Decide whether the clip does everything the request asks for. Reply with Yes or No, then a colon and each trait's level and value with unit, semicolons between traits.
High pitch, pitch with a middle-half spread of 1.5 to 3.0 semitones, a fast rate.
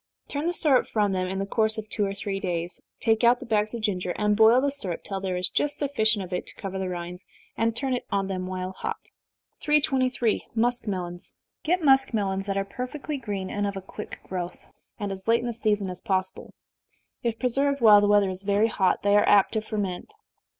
No: high, 205 Hz; average, 3.8 semitones; fast, 220 wpm